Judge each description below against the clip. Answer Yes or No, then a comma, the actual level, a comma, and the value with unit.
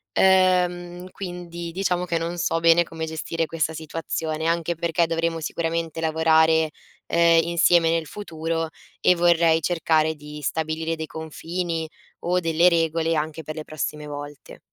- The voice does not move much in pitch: Yes, narrow, 1.3 semitones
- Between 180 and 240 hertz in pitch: No, medium, 165 Hz